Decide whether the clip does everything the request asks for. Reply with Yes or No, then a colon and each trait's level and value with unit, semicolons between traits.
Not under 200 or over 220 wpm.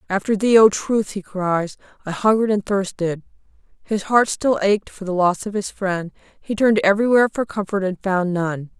No: average, 190 wpm